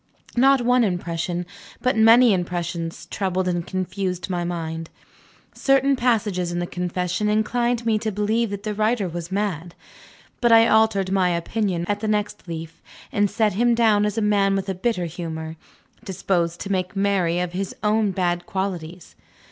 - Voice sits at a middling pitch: No, high, 195 Hz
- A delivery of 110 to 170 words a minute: Yes, average, 165 wpm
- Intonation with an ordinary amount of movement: Yes, average, 3.8 semitones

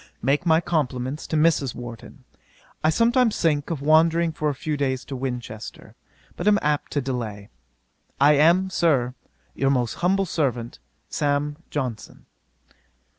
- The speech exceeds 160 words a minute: No, average, 140 wpm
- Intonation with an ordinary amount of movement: Yes, average, 4.2 semitones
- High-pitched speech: No, medium, 145 Hz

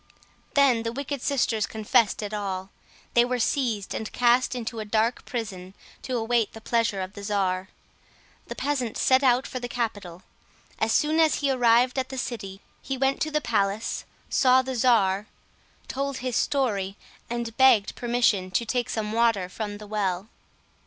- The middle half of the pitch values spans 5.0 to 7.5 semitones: No, average, 3.7 semitones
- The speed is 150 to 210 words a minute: Yes, average, 170 wpm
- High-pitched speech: Yes, high, 230 Hz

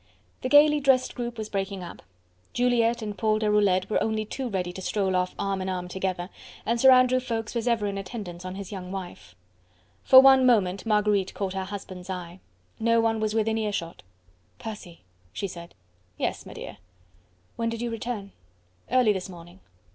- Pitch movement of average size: Yes, average, 3.7 semitones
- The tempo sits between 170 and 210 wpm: Yes, average, 175 wpm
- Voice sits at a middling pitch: No, high, 210 Hz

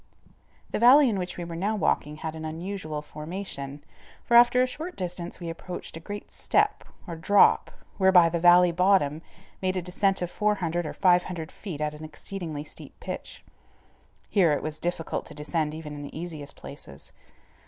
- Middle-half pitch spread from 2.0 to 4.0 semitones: Yes, average, 3.6 semitones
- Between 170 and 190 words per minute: Yes, average, 175 wpm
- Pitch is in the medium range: Yes, medium, 175 Hz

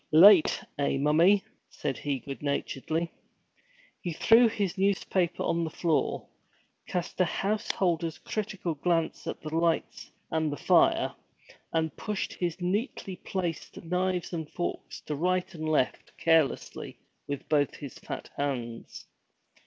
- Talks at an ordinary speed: No, slow, 130 wpm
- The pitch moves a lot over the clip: No, average, 3.5 semitones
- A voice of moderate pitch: Yes, medium, 165 Hz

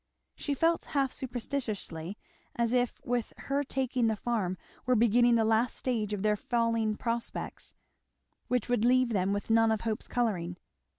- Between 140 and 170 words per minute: Yes, average, 160 wpm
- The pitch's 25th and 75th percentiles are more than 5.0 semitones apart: No, average, 2.7 semitones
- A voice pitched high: Yes, high, 230 Hz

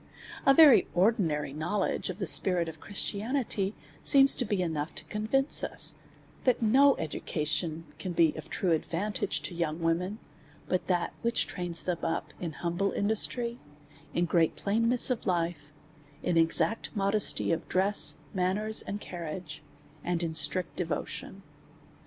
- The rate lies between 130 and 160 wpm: Yes, average, 150 wpm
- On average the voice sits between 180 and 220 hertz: Yes, medium, 185 Hz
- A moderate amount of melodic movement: Yes, average, 4.3 semitones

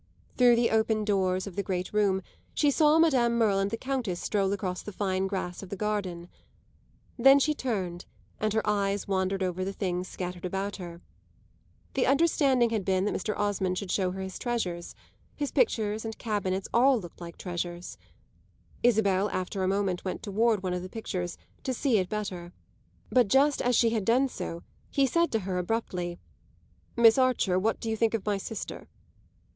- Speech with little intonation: No, average, 3.9 semitones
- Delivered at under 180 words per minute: No, average, 185 wpm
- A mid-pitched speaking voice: No, high, 200 Hz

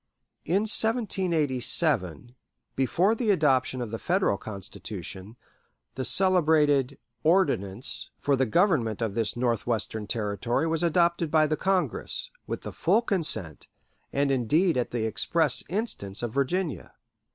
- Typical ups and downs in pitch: No, wide, 7.4 semitones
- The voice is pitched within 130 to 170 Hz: Yes, medium, 140 Hz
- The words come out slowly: Yes, slow, 125 wpm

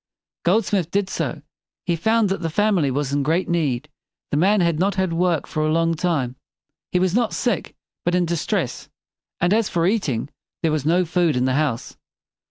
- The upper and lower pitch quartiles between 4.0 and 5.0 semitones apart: No, average, 3.6 semitones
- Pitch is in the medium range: Yes, medium, 170 Hz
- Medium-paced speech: Yes, average, 190 wpm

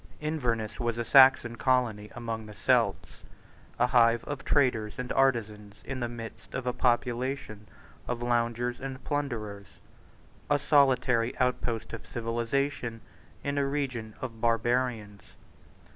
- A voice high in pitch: No, low, 120 Hz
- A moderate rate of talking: No, slow, 130 wpm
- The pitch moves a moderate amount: No, narrow, 2.3 semitones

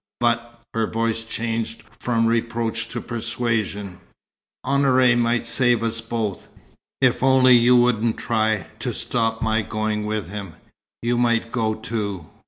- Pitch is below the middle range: Yes, low, 115 Hz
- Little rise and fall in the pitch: Yes, narrow, 1.5 semitones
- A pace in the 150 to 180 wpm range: No, slow, 135 wpm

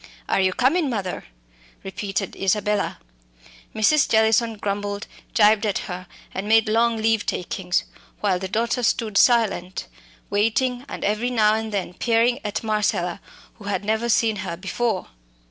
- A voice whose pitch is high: Yes, high, 215 Hz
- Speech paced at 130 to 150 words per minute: Yes, average, 145 wpm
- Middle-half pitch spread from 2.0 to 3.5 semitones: Yes, narrow, 2.5 semitones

